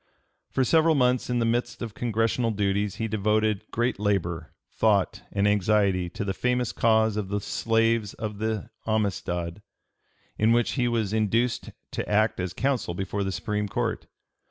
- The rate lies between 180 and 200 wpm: No, average, 160 wpm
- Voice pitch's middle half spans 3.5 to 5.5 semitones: No, narrow, 2.5 semitones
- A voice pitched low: Yes, low, 110 Hz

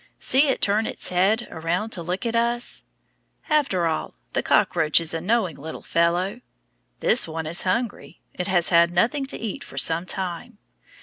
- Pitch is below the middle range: No, medium, 185 Hz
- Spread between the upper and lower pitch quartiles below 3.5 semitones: No, wide, 5.5 semitones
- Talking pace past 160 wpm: Yes, average, 175 wpm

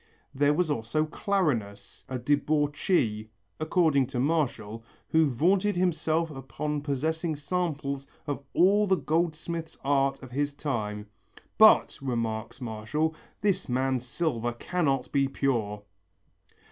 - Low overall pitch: No, medium, 145 Hz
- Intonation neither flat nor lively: Yes, average, 4.6 semitones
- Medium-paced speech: No, slow, 115 wpm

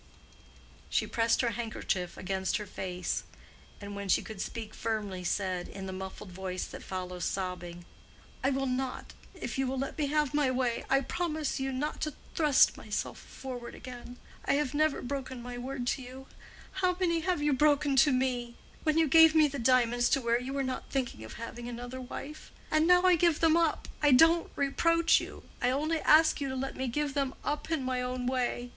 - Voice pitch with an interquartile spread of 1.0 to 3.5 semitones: No, average, 4.2 semitones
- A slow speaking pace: No, average, 190 wpm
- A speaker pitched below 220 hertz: No, very high, 260 Hz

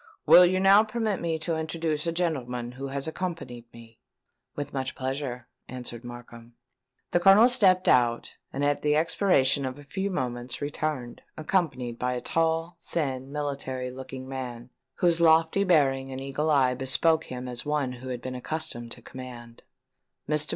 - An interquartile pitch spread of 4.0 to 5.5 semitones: Yes, average, 4.5 semitones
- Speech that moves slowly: No, average, 165 wpm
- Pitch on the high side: No, medium, 140 Hz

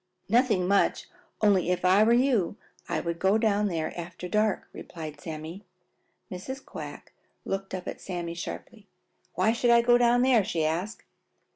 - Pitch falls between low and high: No, high, 195 Hz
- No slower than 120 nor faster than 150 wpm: No, average, 160 wpm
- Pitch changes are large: No, average, 4.5 semitones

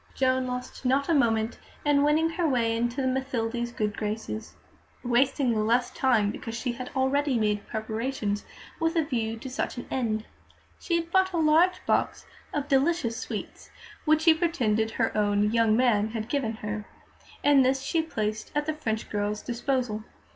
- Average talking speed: Yes, average, 170 wpm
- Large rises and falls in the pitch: No, average, 4.5 semitones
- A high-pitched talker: Yes, high, 245 Hz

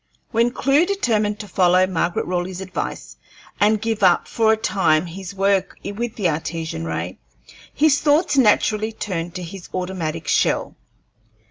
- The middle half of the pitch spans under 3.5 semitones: No, average, 4.0 semitones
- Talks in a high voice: Yes, high, 195 Hz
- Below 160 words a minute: Yes, average, 145 wpm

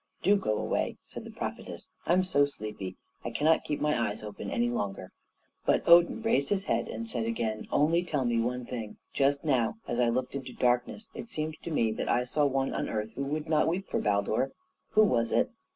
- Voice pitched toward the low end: Yes, low, 130 Hz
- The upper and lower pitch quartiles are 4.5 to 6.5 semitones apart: Yes, average, 5.3 semitones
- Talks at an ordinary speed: No, fast, 215 wpm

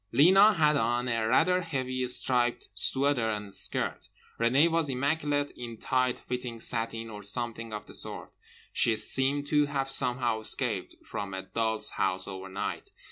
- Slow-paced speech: No, average, 150 wpm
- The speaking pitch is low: Yes, low, 125 Hz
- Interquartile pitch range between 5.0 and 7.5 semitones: No, average, 4.2 semitones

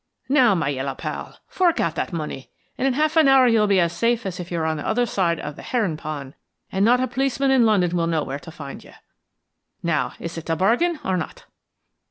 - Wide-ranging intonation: Yes, wide, 7.3 semitones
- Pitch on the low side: No, medium, 185 Hz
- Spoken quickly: Yes, fast, 240 wpm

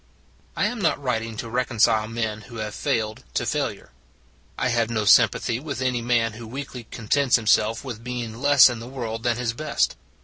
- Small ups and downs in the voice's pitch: Yes, narrow, 2.1 semitones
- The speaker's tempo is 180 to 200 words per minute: Yes, average, 190 wpm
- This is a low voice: Yes, low, 115 Hz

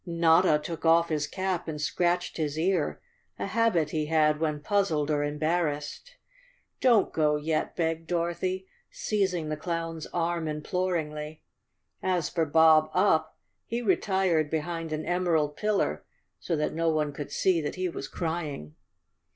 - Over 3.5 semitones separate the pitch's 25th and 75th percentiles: No, average, 2.9 semitones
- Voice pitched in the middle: Yes, medium, 165 Hz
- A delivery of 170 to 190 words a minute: No, average, 145 wpm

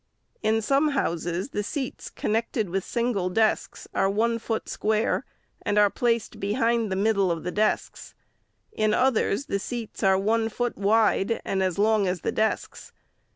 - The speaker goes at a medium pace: Yes, average, 165 wpm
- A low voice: No, high, 215 Hz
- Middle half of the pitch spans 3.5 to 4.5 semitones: No, average, 2.8 semitones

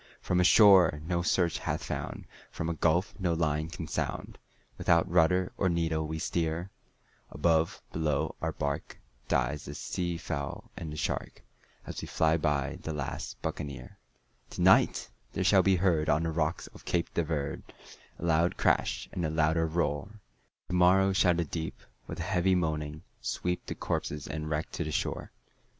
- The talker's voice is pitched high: No, very low, 80 Hz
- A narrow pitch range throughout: Yes, narrow, 2.3 semitones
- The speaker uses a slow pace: No, average, 175 wpm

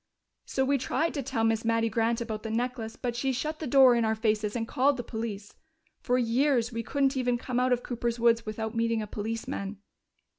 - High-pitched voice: Yes, high, 235 Hz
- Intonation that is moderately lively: No, narrow, 2.2 semitones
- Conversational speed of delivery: No, fast, 215 wpm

